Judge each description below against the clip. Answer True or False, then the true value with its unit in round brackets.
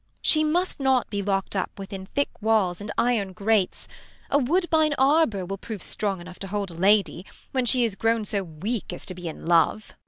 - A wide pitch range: False (4.7 semitones)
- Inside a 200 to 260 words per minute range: True (205 wpm)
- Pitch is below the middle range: False (205 Hz)